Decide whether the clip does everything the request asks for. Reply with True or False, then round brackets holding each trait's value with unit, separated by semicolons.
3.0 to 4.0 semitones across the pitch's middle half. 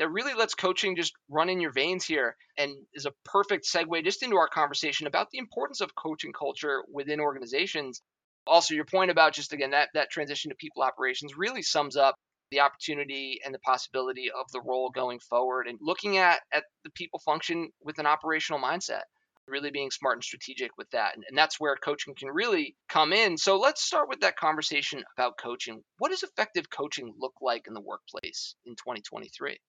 False (4.6 semitones)